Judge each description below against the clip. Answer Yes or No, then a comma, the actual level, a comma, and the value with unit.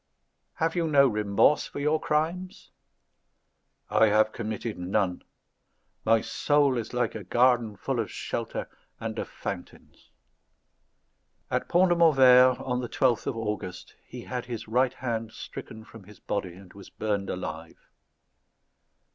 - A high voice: No, low, 115 Hz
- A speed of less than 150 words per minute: Yes, average, 140 wpm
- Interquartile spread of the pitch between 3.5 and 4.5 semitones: Yes, average, 4.1 semitones